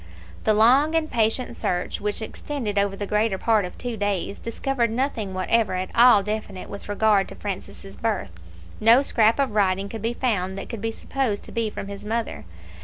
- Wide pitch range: No, average, 2.7 semitones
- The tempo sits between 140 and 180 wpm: No, average, 190 wpm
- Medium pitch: No, high, 215 Hz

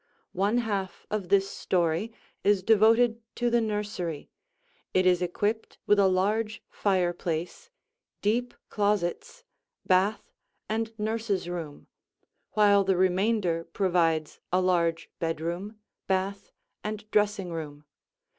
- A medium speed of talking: No, slow, 110 wpm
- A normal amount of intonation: Yes, average, 3.3 semitones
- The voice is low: No, high, 195 Hz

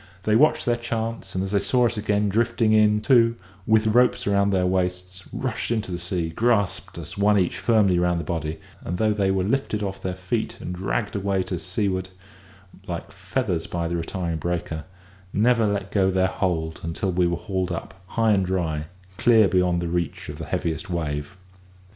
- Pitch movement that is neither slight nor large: Yes, average, 3.5 semitones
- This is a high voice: No, very low, 95 Hz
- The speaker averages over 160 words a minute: Yes, average, 190 wpm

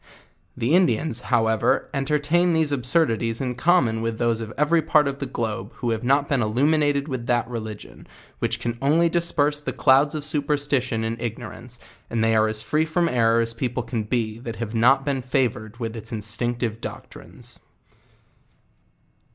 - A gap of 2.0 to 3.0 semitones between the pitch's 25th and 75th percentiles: No, average, 4.3 semitones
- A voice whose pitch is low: Yes, low, 125 Hz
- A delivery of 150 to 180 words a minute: Yes, average, 170 wpm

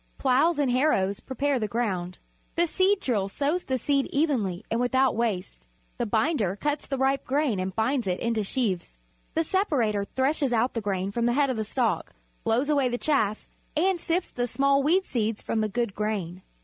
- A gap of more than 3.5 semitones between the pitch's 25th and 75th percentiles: Yes, average, 5.2 semitones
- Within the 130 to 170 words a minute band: No, average, 190 wpm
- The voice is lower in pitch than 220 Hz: No, high, 245 Hz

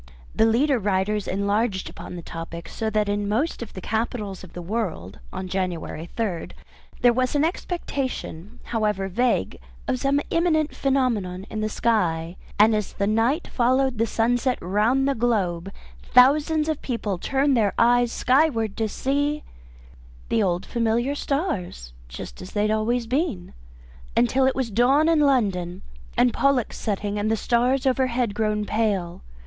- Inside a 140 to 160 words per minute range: Yes, average, 155 wpm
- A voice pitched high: Yes, high, 225 Hz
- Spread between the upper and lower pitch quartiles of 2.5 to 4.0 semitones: No, average, 4.6 semitones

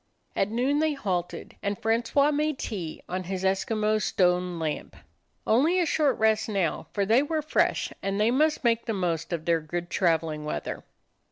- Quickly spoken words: No, average, 175 wpm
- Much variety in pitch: Yes, wide, 6.3 semitones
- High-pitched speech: Yes, high, 210 Hz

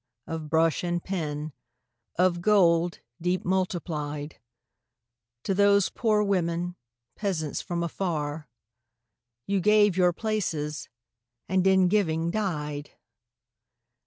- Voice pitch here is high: No, medium, 175 Hz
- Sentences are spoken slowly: Yes, slow, 100 wpm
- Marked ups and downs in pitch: No, average, 3.4 semitones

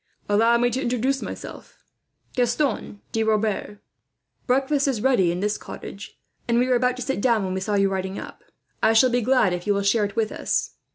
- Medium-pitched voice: No, high, 225 Hz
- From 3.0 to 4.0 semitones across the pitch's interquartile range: Yes, average, 3.7 semitones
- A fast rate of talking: Yes, fast, 215 wpm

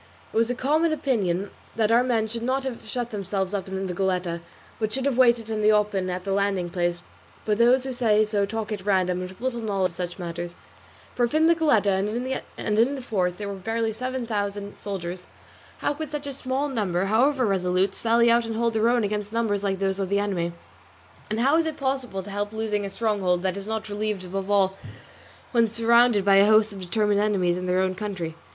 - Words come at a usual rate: No, fast, 225 wpm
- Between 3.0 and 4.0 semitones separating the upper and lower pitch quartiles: Yes, average, 3.5 semitones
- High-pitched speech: Yes, high, 210 Hz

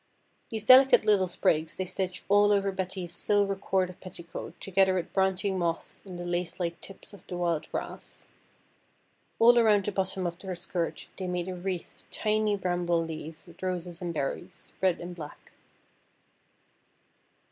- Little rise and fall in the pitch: Yes, narrow, 2.1 semitones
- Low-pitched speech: No, medium, 185 Hz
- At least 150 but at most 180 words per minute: Yes, average, 160 wpm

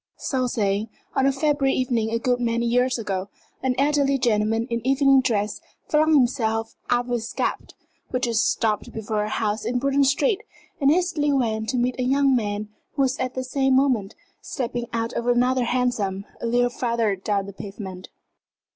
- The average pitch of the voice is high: Yes, high, 245 Hz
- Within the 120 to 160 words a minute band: No, average, 185 wpm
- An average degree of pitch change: Yes, average, 3.4 semitones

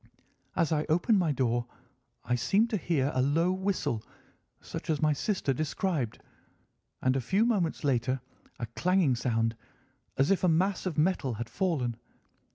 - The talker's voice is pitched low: No, medium, 155 Hz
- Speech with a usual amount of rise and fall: No, wide, 6.6 semitones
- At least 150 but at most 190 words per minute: Yes, average, 160 wpm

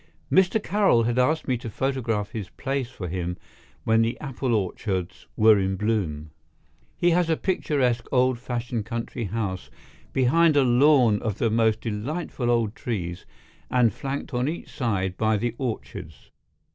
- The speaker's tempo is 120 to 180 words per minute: Yes, average, 155 wpm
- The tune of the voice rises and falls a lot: No, average, 4.2 semitones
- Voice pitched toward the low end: Yes, low, 115 Hz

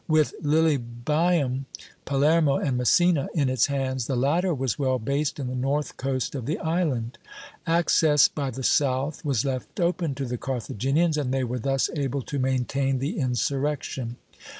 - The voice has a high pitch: No, low, 135 Hz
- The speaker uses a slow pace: No, average, 160 wpm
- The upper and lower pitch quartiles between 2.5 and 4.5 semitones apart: Yes, average, 2.8 semitones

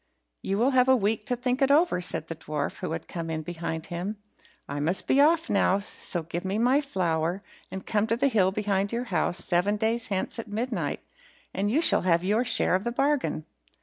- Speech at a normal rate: No, fast, 220 wpm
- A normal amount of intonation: No, wide, 5.9 semitones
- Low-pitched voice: No, high, 205 Hz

